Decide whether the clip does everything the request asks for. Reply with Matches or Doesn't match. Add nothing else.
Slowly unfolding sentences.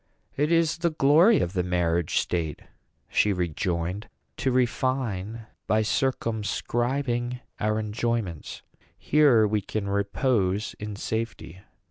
Matches